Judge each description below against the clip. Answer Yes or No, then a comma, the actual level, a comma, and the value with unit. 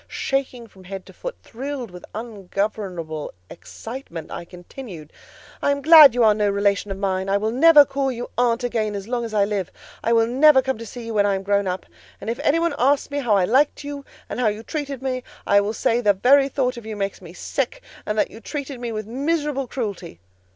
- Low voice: No, high, 230 Hz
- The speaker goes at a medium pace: No, fast, 230 wpm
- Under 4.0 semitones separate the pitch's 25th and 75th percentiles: No, average, 5.1 semitones